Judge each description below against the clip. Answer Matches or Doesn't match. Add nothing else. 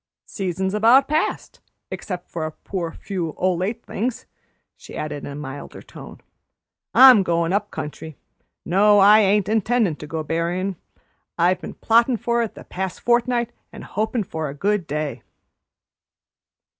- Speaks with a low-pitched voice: Doesn't match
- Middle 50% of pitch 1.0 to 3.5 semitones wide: Doesn't match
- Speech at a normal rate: Matches